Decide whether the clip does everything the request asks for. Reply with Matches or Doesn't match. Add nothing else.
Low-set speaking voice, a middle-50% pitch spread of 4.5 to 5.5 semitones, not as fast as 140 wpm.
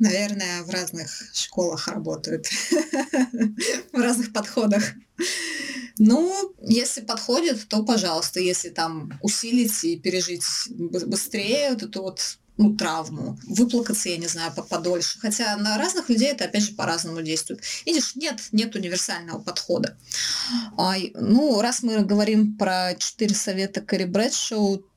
Doesn't match